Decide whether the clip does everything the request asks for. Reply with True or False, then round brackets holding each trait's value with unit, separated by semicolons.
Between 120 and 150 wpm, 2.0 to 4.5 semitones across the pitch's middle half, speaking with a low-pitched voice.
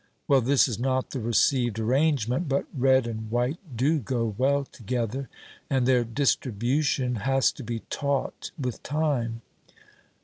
True (140 wpm; 2.8 semitones; 130 Hz)